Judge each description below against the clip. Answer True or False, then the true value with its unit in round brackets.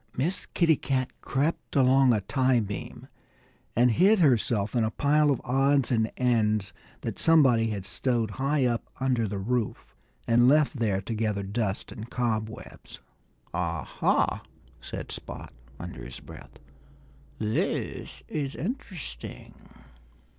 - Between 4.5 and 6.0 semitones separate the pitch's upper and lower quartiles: False (4.1 semitones)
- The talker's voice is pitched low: True (120 Hz)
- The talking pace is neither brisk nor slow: False (130 wpm)